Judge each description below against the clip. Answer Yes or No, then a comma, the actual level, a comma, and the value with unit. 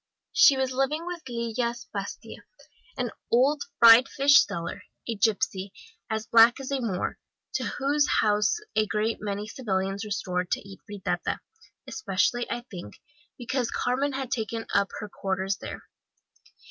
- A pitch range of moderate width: Yes, average, 4.5 semitones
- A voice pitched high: Yes, high, 230 Hz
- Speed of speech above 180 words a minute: No, average, 145 wpm